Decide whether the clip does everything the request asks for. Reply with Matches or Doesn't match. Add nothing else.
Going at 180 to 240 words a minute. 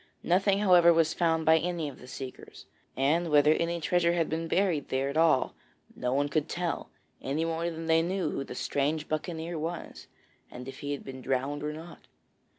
Matches